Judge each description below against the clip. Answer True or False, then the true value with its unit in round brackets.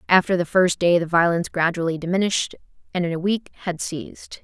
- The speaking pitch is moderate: True (175 Hz)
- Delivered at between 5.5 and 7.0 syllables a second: True (6.2 syllables/s)